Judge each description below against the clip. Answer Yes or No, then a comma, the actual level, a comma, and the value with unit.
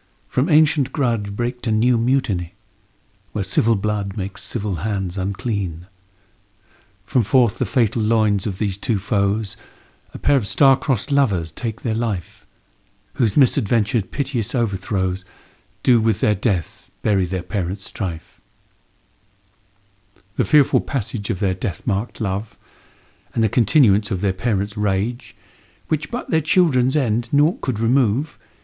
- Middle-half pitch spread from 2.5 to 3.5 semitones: No, average, 3.9 semitones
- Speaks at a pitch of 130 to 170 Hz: No, low, 105 Hz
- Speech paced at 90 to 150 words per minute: Yes, average, 140 wpm